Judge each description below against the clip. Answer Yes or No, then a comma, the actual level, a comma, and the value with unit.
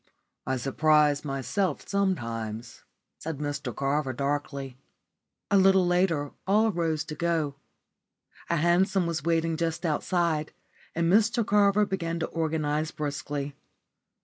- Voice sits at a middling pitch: Yes, medium, 160 Hz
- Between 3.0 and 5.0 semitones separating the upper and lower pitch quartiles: Yes, average, 3.5 semitones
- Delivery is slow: Yes, slow, 120 wpm